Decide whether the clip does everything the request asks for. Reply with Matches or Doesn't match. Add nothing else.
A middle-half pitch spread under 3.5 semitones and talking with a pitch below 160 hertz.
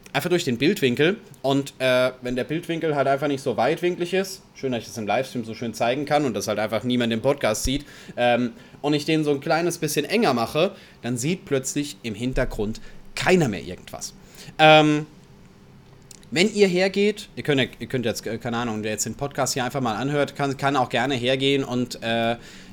Doesn't match